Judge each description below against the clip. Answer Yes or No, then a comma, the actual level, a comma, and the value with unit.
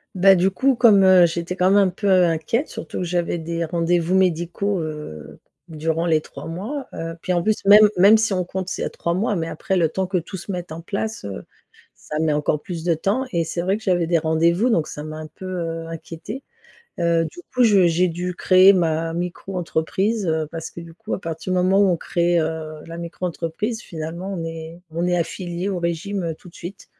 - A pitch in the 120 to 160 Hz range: No, medium, 175 Hz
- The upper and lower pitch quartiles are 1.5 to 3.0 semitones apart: Yes, narrow, 2.6 semitones